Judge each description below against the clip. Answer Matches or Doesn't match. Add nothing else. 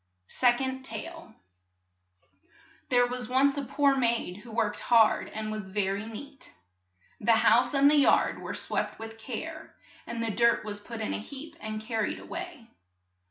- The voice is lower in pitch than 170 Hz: Doesn't match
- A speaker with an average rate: Matches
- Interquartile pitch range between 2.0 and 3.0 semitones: Doesn't match